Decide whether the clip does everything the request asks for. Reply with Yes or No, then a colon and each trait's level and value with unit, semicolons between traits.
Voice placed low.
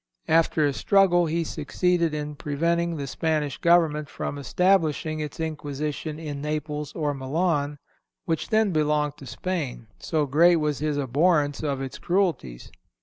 No: medium, 150 Hz